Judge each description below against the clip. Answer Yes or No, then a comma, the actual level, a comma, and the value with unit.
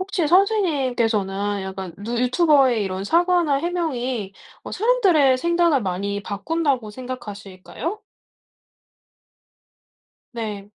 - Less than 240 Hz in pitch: No, very high, 255 Hz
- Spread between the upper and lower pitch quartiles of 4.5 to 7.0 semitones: No, wide, 8.8 semitones